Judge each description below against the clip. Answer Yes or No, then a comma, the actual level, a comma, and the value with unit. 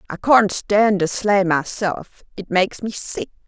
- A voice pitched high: Yes, high, 195 Hz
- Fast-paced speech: No, average, 170 wpm